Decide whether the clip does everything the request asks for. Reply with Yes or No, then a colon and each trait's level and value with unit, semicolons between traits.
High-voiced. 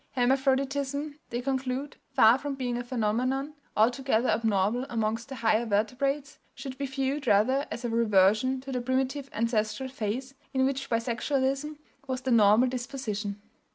Yes: very high, 255 Hz